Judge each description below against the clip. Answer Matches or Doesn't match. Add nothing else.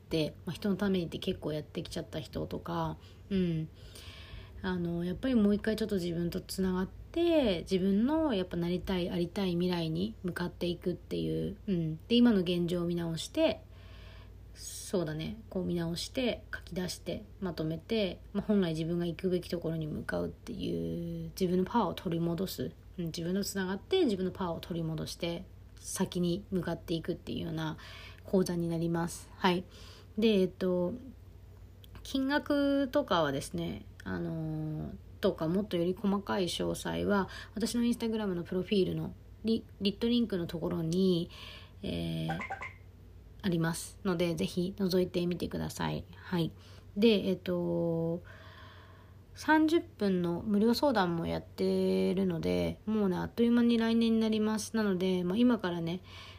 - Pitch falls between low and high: Matches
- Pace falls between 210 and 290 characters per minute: Doesn't match